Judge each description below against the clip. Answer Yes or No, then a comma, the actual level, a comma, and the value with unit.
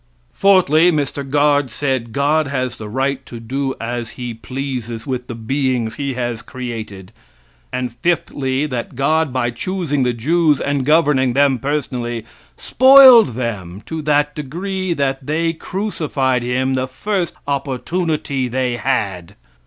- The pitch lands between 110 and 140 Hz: Yes, low, 135 Hz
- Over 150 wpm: No, slow, 135 wpm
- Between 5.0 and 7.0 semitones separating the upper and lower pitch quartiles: No, average, 3.7 semitones